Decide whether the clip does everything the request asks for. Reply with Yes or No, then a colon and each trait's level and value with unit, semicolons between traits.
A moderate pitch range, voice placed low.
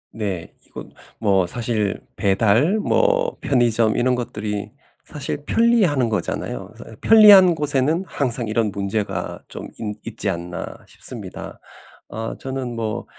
No: wide, 5.8 semitones; low, 115 Hz